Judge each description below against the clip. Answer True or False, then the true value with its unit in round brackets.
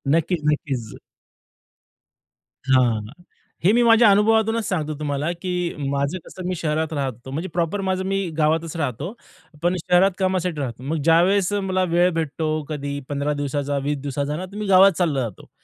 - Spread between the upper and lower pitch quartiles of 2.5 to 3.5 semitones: False (4.7 semitones)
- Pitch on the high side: False (165 Hz)